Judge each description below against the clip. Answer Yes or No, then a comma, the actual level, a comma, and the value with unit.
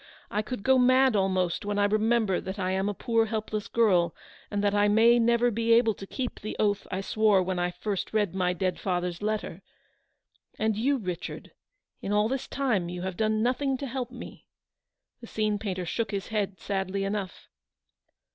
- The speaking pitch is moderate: No, high, 210 Hz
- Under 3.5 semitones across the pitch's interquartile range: Yes, average, 3.1 semitones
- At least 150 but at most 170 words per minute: No, average, 190 wpm